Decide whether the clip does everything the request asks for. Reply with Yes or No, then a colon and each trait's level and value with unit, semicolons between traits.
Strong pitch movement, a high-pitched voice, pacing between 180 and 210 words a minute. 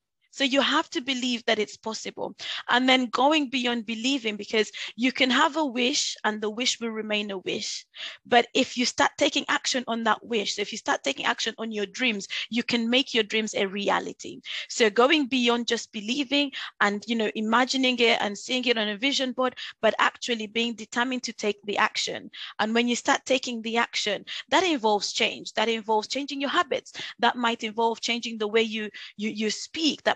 No: average, 3.1 semitones; high, 235 Hz; fast, 205 wpm